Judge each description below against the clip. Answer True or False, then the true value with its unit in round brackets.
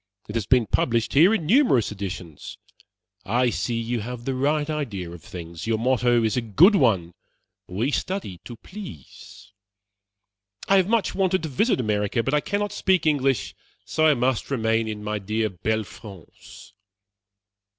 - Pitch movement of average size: False (6.4 semitones)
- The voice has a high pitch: False (120 Hz)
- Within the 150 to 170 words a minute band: True (160 wpm)